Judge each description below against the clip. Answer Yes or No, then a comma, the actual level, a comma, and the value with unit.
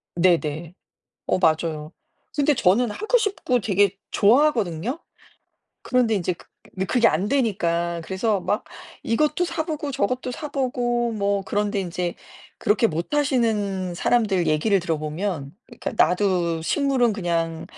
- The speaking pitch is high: Yes, high, 200 Hz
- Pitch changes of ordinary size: No, wide, 6.2 semitones